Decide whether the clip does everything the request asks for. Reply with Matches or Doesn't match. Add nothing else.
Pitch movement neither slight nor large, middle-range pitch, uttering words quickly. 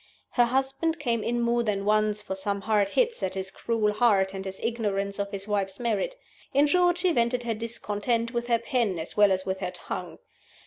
Doesn't match